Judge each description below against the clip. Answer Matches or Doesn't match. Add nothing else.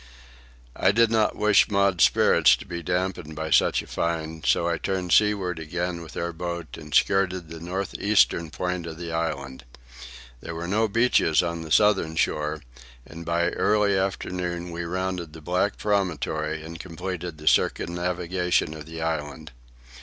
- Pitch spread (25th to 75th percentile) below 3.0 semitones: Matches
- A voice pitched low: Matches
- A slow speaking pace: Doesn't match